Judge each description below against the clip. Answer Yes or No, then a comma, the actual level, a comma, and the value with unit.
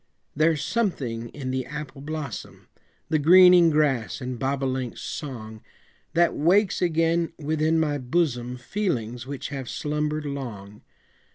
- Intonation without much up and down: No, average, 4.2 semitones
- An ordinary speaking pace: No, slow, 120 wpm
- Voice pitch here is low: No, medium, 145 Hz